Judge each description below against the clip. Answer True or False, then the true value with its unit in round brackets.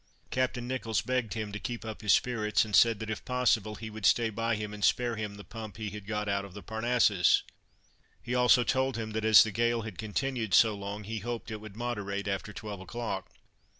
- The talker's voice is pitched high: False (110 Hz)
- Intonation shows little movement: True (2.2 semitones)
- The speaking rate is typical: False (225 wpm)